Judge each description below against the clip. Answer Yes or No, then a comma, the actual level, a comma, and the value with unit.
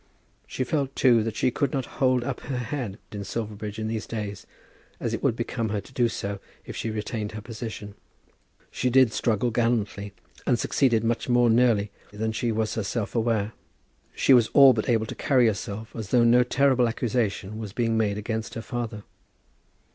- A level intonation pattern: Yes, narrow, 2.3 semitones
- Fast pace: No, average, 185 wpm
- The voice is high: No, low, 115 Hz